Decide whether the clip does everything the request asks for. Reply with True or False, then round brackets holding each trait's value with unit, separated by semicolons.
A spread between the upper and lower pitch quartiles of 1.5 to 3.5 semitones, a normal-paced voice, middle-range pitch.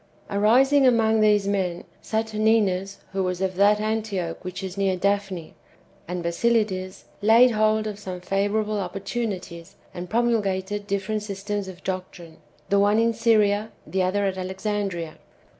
False (2.5 semitones; 145 wpm; 200 Hz)